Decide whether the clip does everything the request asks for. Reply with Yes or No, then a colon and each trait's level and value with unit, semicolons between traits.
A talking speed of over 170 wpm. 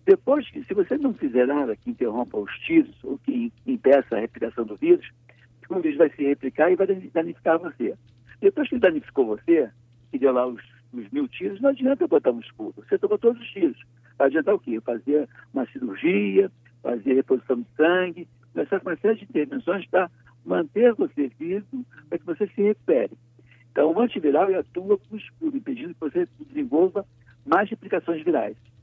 Yes: average, 180 wpm